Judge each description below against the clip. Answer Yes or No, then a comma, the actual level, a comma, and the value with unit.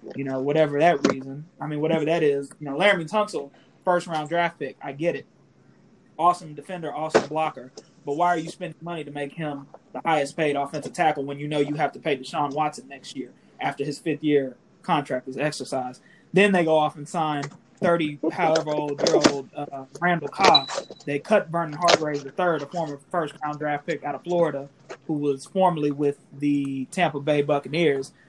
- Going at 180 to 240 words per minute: Yes, average, 200 wpm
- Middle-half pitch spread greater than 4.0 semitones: No, average, 2.9 semitones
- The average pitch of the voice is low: No, medium, 150 Hz